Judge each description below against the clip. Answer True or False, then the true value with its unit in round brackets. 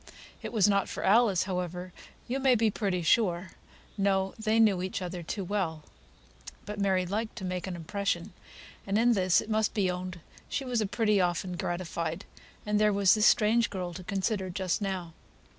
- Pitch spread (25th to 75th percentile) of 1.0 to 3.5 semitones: True (2.8 semitones)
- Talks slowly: False (175 wpm)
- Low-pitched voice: False (195 Hz)